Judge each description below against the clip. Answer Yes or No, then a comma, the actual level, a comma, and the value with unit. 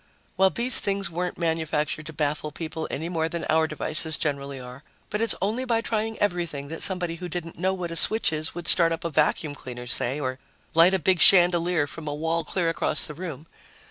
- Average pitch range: Yes, average, 3.0 semitones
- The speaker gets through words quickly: Yes, fast, 210 wpm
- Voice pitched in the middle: Yes, medium, 165 Hz